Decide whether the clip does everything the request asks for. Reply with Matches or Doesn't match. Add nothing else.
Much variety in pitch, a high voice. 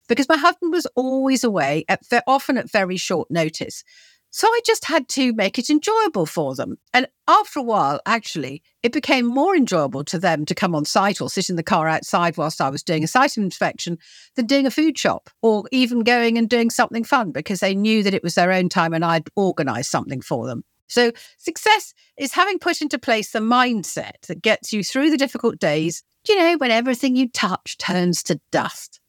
Matches